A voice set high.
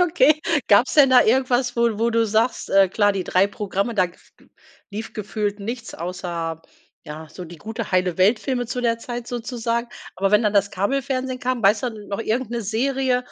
Yes: high, 225 Hz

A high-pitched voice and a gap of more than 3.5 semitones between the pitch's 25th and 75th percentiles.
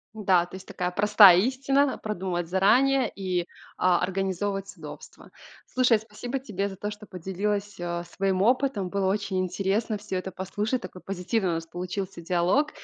No: high, 195 Hz; average, 2.7 semitones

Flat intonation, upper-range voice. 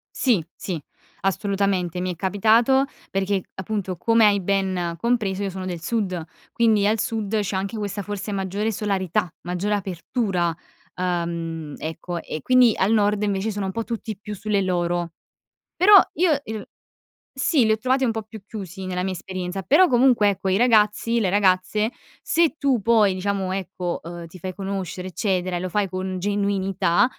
No: average, 3.0 semitones; high, 195 Hz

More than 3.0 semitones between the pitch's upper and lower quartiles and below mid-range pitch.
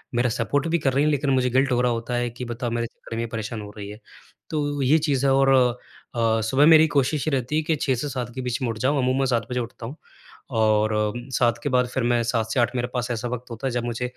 No: average, 2.7 semitones; low, 125 Hz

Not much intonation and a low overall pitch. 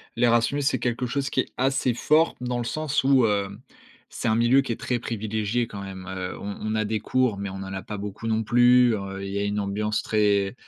No: average, 3.5 semitones; low, 110 Hz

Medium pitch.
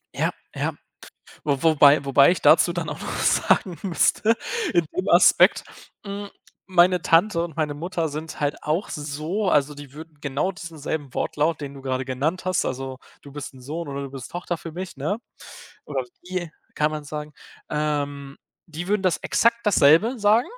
Yes: medium, 155 Hz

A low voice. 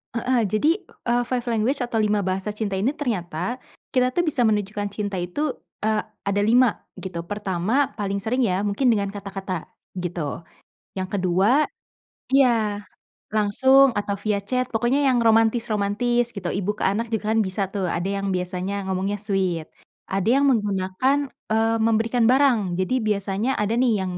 No: high, 210 Hz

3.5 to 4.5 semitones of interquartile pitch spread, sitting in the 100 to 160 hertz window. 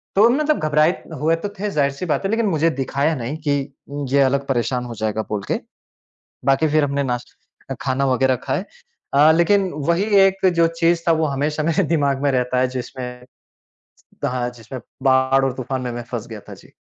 Yes: average, 4.0 semitones; medium, 140 Hz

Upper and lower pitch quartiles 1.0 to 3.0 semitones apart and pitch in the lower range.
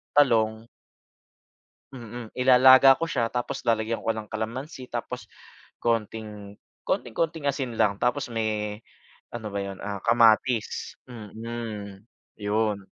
Yes: average, 2.7 semitones; low, 115 Hz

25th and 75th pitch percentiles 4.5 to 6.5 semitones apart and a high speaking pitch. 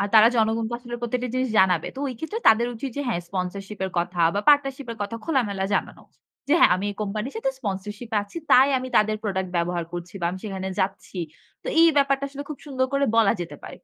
Yes: average, 5.3 semitones; high, 220 Hz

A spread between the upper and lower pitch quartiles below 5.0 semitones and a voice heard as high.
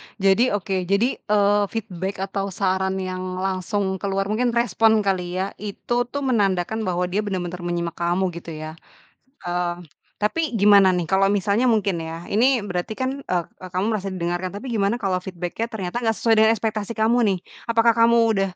Yes: average, 3.3 semitones; high, 195 Hz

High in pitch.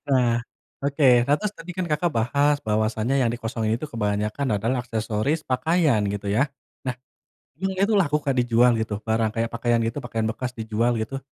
No: low, 120 Hz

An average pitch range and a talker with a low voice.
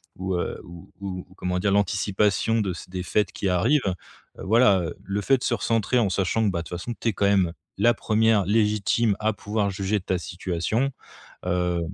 Yes: average, 3.2 semitones; low, 100 Hz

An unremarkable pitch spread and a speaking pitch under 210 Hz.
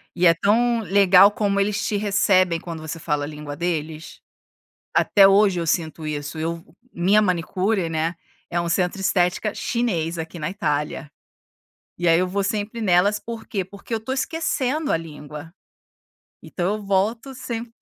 Yes: average, 4.2 semitones; medium, 185 Hz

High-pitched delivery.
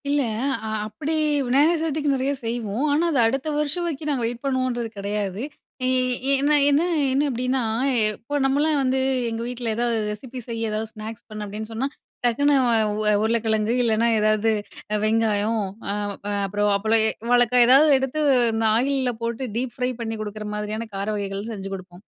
Yes: high, 230 Hz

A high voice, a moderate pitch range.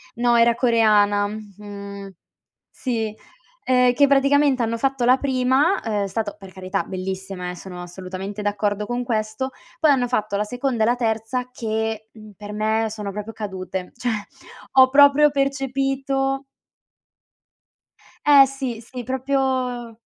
Yes: high, 230 Hz; average, 4.1 semitones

